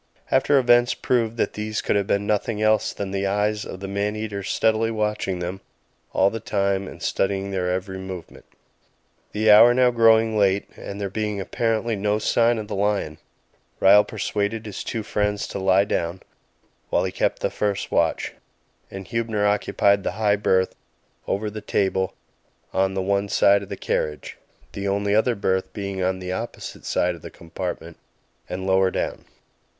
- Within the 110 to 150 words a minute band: No, average, 175 wpm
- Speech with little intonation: Yes, narrow, 2.1 semitones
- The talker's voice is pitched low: Yes, low, 100 Hz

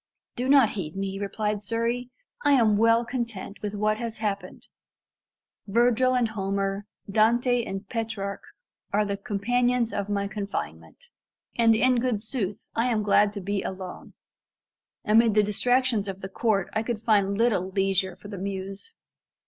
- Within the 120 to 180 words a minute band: Yes, average, 155 wpm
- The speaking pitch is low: No, high, 210 Hz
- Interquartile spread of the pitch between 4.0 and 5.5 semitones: No, average, 2.9 semitones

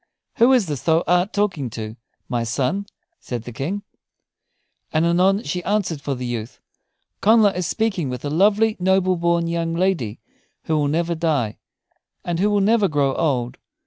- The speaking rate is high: No, average, 170 wpm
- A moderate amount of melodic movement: No, wide, 5.9 semitones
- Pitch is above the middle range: No, medium, 170 Hz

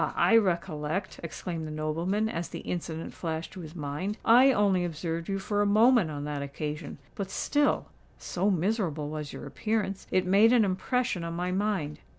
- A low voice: No, medium, 180 Hz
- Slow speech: No, average, 165 wpm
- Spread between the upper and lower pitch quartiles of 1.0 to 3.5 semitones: No, average, 4.7 semitones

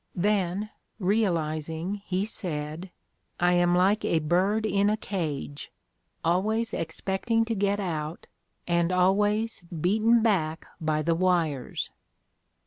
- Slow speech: Yes, slow, 115 wpm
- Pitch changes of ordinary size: Yes, average, 4.1 semitones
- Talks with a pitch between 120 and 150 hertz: No, medium, 185 Hz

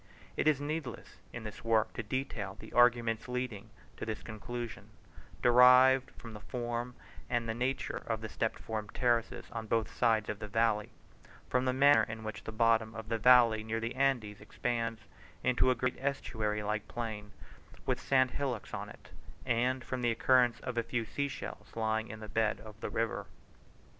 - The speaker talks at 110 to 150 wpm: No, average, 185 wpm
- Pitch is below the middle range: Yes, low, 115 Hz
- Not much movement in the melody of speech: Yes, narrow, 2.3 semitones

